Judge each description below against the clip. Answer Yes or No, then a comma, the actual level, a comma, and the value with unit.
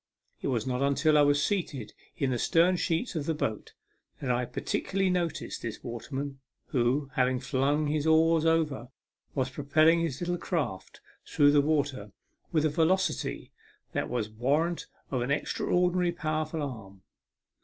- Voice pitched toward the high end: No, medium, 145 Hz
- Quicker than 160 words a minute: No, average, 155 wpm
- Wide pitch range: No, average, 4.1 semitones